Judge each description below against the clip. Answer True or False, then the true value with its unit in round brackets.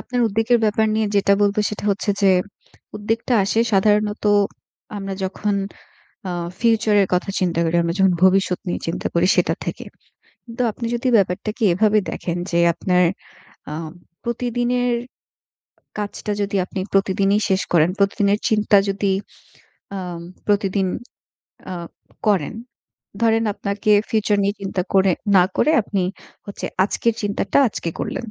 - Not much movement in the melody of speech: True (2.2 semitones)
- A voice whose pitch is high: True (205 Hz)